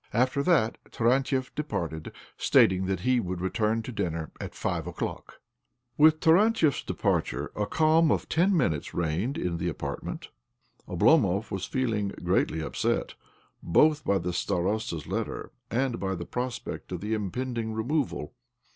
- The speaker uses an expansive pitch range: Yes, wide, 6.7 semitones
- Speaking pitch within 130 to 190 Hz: No, low, 110 Hz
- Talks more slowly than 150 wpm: Yes, average, 140 wpm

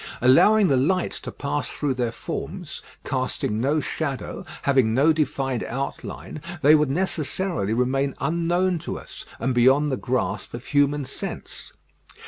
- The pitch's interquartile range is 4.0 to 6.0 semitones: No, average, 3.4 semitones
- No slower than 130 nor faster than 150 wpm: Yes, average, 140 wpm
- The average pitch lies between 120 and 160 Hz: Yes, medium, 140 Hz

